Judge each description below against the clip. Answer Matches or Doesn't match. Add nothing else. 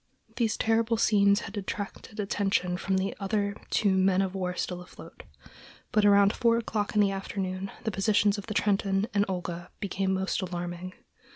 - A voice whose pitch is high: Matches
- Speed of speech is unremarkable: Matches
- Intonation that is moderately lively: Doesn't match